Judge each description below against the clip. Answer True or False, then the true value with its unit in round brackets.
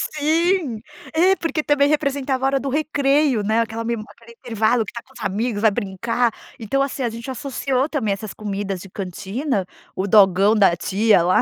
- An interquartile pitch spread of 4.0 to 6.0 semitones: True (5.2 semitones)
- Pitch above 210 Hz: True (235 Hz)